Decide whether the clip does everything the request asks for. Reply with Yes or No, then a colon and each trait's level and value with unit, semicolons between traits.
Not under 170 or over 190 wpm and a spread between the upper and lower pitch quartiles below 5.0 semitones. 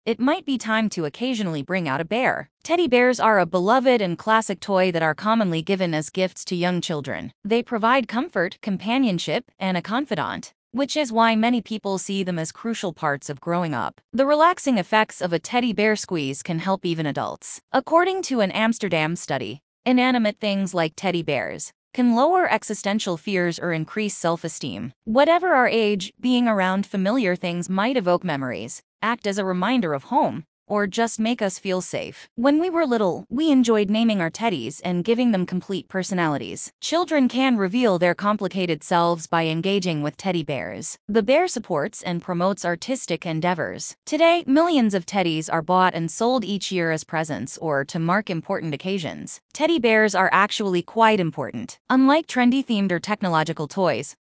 No: average, 175 wpm; average, 5.3 semitones